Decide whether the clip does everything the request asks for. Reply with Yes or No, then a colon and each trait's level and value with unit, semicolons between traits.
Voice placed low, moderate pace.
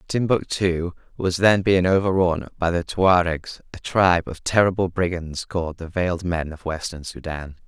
Yes: very low, 90 Hz; average, 155 wpm